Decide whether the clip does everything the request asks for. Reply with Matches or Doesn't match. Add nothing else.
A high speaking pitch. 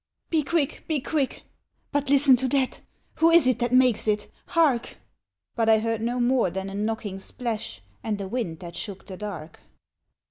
Matches